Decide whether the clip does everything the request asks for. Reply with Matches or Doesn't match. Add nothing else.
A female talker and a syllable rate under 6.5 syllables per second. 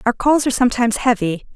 Doesn't match